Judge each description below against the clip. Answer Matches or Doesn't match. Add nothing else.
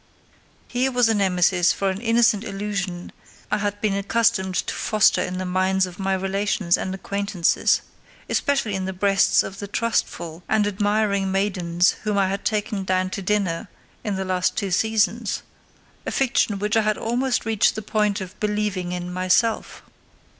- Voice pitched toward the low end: Doesn't match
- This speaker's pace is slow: Doesn't match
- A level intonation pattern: Matches